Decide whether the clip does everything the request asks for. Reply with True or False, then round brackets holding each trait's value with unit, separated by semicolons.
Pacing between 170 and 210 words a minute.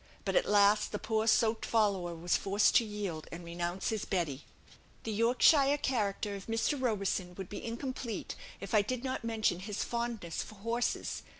True (175 wpm)